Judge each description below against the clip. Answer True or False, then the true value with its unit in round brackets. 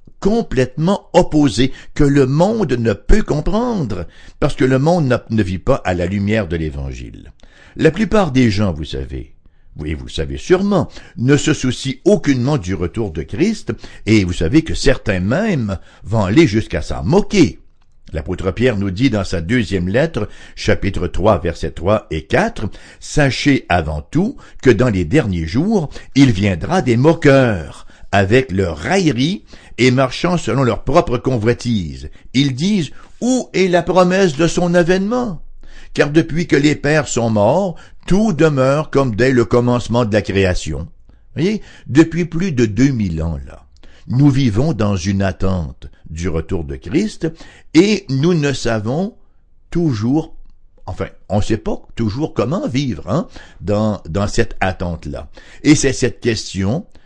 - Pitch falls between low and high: False (125 Hz)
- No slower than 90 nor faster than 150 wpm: False (160 wpm)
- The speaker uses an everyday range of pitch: False (8.6 semitones)